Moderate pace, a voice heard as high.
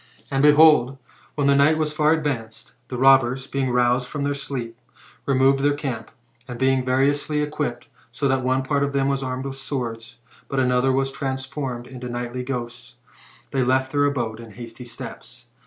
No: average, 175 wpm; low, 130 Hz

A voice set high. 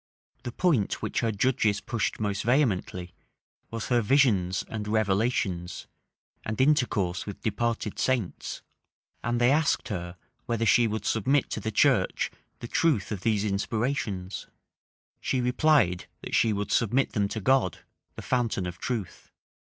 No: low, 110 Hz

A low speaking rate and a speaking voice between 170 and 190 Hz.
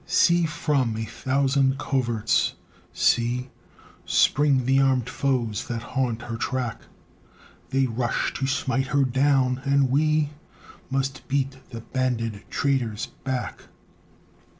No: slow, 115 wpm; low, 130 Hz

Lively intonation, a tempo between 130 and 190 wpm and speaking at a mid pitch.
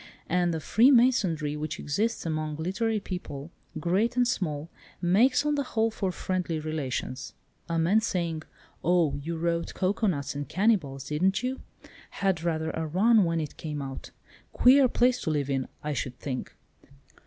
Yes: wide, 6.0 semitones; average, 155 wpm; medium, 170 Hz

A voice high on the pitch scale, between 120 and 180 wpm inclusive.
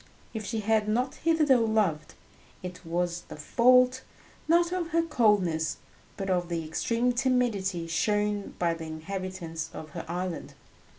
Yes: high, 205 Hz; average, 140 wpm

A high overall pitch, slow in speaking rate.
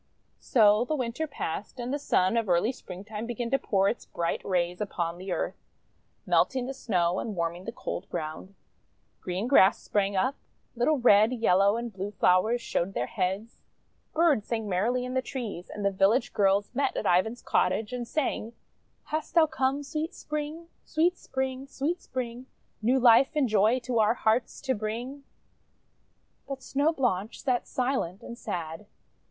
No: high, 230 Hz; average, 170 wpm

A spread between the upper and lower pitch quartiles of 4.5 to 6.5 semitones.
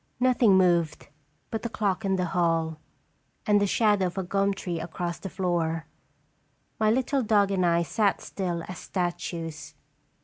No: average, 3.1 semitones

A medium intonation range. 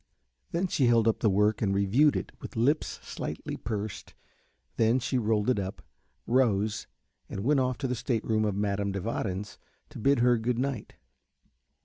Yes: average, 3.6 semitones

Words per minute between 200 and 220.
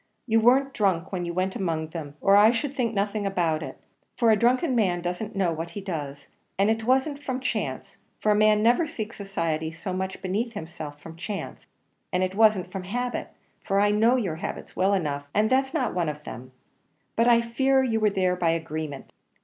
Yes: fast, 205 wpm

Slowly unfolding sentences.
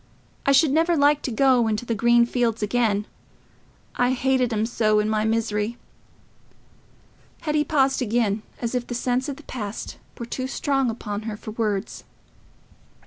No: average, 155 wpm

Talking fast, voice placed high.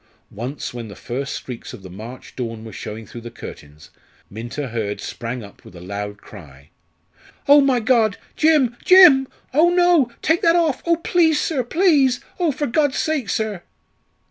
No: average, 170 wpm; high, 215 Hz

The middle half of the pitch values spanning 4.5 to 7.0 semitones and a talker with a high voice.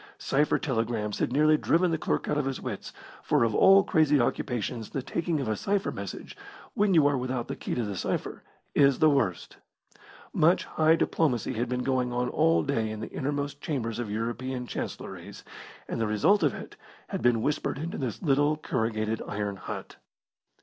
No: average, 4.9 semitones; low, 130 Hz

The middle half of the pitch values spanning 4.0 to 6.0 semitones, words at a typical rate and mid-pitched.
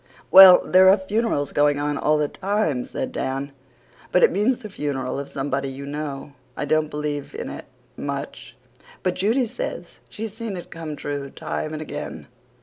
Yes: average, 5.1 semitones; average, 175 wpm; medium, 150 Hz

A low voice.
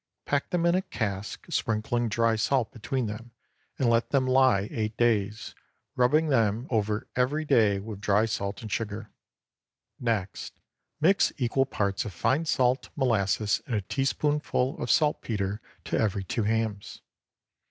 Yes: low, 115 Hz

